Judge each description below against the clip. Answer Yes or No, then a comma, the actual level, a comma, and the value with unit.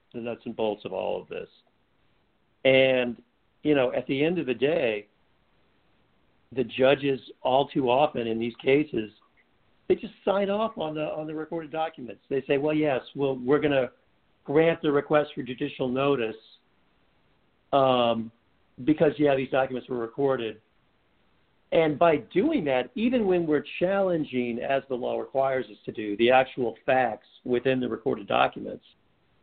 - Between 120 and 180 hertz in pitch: Yes, low, 135 Hz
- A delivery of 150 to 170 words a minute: Yes, average, 160 wpm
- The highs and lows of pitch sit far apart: No, average, 4.0 semitones